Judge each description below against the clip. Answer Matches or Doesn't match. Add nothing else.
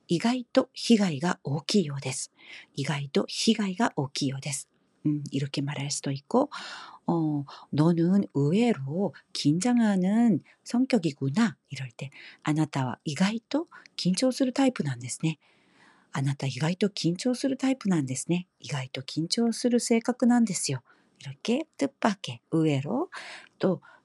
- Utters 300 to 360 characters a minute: Doesn't match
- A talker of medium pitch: Matches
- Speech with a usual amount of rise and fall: Doesn't match